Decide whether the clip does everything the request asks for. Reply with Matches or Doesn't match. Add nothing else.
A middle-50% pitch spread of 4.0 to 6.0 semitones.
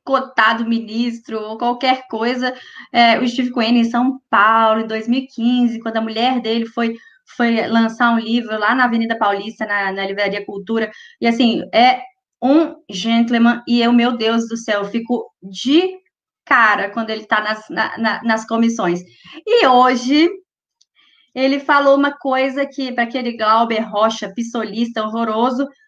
Doesn't match